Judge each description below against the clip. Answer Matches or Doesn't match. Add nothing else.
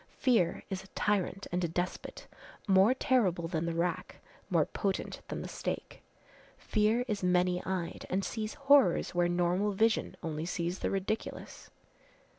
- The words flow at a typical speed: Matches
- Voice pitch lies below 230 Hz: Matches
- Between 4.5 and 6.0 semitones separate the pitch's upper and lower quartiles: Doesn't match